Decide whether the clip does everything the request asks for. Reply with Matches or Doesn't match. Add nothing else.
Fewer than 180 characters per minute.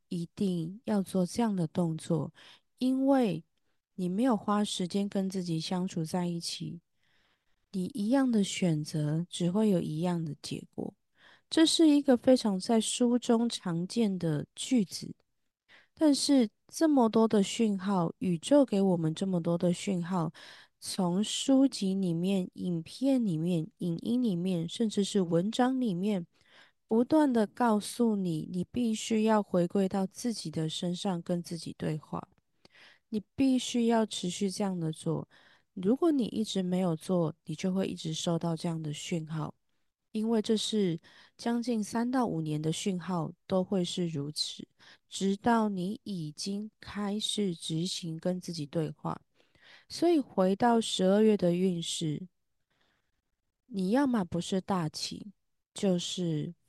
Doesn't match